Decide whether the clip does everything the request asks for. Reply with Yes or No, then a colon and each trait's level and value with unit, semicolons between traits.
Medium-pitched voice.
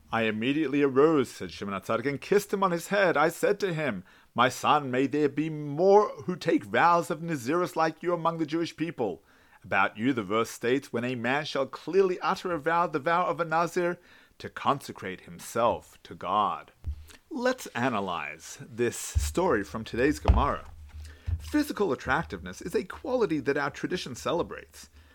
Yes: medium, 155 Hz